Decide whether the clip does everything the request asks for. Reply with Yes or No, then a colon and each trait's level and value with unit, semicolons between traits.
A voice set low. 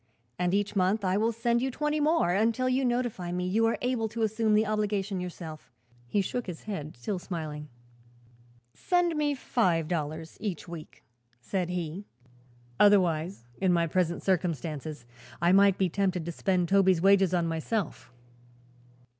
No: high, 190 Hz